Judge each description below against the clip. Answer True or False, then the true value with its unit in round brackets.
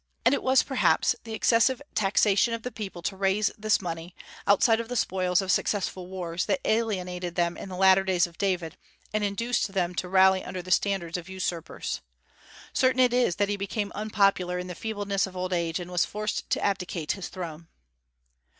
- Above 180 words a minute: True (195 wpm)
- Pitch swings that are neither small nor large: True (3.0 semitones)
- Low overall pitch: False (190 Hz)